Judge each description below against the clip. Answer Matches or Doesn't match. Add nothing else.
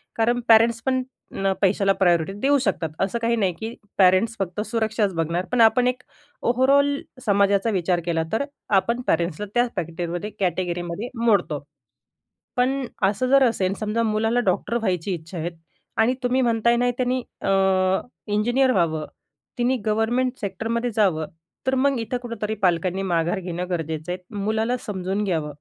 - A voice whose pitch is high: Matches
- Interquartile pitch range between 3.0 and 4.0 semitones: Doesn't match